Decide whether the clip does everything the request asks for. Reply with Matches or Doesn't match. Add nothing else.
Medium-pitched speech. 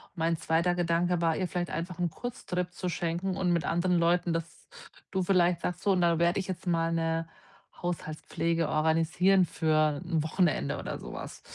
Matches